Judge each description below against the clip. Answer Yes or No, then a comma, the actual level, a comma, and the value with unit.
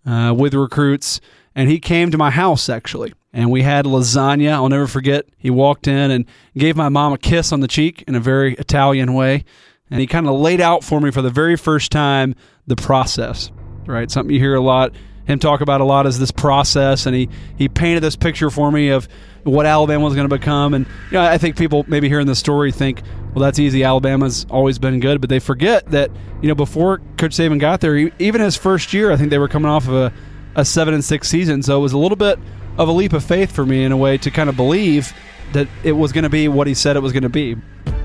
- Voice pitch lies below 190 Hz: Yes, medium, 140 Hz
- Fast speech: Yes, fast, 250 wpm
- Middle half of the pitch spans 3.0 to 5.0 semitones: No, narrow, 2.5 semitones